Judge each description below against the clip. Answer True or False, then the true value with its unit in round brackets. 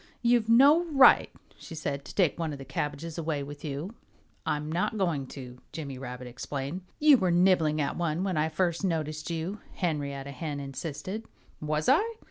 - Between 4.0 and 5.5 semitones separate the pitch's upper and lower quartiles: True (4.7 semitones)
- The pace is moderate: True (175 wpm)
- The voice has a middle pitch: True (155 Hz)